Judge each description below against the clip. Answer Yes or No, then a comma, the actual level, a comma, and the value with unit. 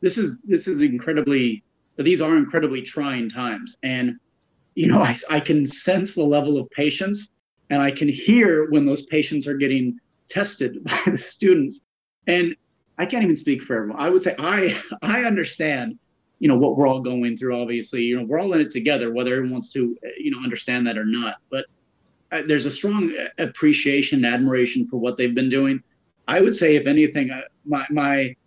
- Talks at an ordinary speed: Yes, average, 195 wpm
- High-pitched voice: No, medium, 140 Hz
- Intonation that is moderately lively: Yes, average, 5.0 semitones